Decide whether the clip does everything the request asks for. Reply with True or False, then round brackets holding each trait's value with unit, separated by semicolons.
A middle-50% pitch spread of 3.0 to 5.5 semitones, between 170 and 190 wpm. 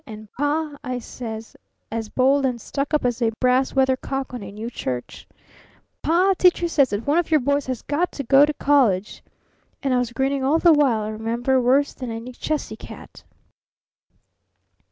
True (3.9 semitones; 180 wpm)